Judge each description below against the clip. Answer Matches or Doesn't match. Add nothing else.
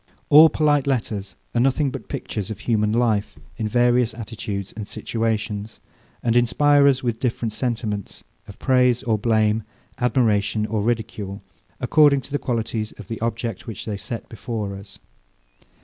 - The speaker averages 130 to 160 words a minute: Matches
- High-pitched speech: Doesn't match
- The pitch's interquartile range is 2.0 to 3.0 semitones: Matches